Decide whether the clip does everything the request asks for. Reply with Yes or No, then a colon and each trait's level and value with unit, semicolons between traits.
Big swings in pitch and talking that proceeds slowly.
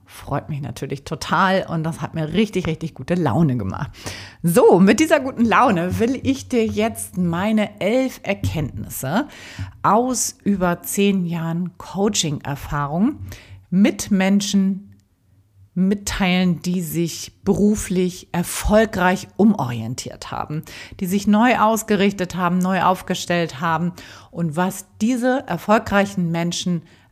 No: average, 4.2 semitones; slow, 115 wpm